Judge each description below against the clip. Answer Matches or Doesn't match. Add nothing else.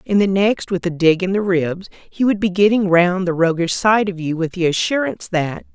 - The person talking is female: Matches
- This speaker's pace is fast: Matches